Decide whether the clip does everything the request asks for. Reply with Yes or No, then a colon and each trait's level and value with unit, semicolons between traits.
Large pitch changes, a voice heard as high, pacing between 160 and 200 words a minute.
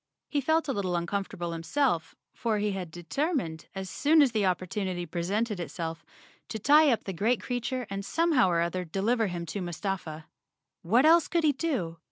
Yes: wide, 6.6 semitones; high, 200 Hz; average, 180 wpm